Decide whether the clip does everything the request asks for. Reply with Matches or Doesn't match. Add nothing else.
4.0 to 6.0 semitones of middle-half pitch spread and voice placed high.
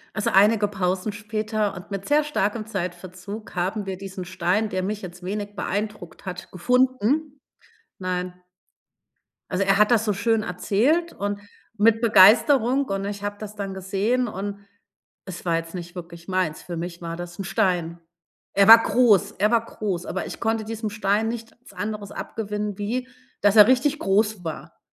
Doesn't match